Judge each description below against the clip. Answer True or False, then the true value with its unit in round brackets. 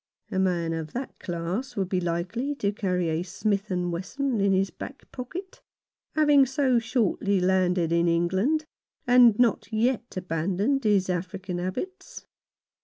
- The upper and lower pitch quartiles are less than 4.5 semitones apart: False (5.5 semitones)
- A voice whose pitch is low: False (195 Hz)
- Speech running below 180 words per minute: True (145 wpm)